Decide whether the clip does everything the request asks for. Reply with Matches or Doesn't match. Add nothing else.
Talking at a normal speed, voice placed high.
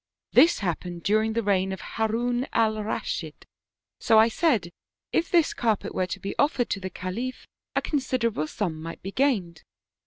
Matches